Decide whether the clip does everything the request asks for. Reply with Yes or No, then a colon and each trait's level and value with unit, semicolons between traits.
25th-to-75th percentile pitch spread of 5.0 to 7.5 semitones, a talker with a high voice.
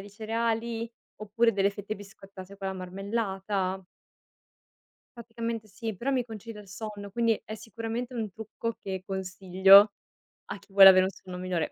No: average, 2.8 semitones; high, 205 Hz